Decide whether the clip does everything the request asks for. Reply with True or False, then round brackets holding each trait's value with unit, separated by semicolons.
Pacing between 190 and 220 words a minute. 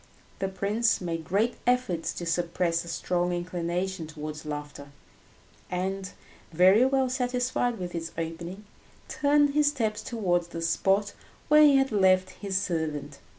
False (140 wpm)